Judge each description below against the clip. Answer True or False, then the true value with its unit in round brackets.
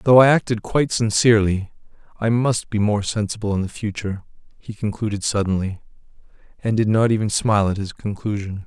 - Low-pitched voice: True (105 Hz)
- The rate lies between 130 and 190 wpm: True (165 wpm)